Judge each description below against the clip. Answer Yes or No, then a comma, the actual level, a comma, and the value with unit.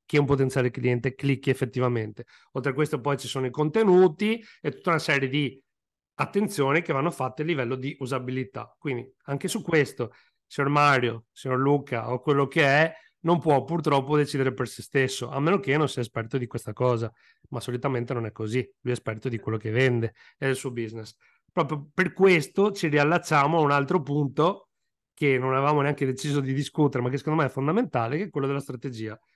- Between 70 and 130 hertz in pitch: No, medium, 140 Hz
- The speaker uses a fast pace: Yes, fast, 200 wpm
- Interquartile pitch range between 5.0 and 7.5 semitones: No, average, 3.2 semitones